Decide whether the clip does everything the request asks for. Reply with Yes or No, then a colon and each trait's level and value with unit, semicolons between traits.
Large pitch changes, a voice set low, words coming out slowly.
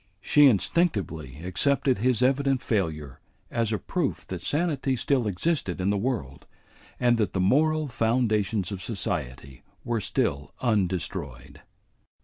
Yes: wide, 6.4 semitones; low, 110 Hz; slow, 130 wpm